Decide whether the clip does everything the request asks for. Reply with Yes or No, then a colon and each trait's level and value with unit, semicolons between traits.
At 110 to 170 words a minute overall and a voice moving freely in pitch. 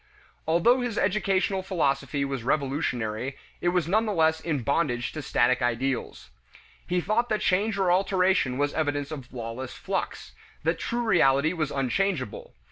Yes: average, 150 wpm; wide, 6.0 semitones